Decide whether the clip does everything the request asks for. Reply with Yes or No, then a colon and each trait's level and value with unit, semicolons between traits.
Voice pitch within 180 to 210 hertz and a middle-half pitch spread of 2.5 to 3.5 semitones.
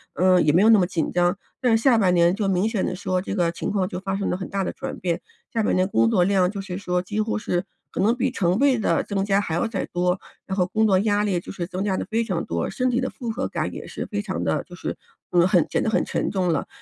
Yes: high, 190 Hz; average, 3.1 semitones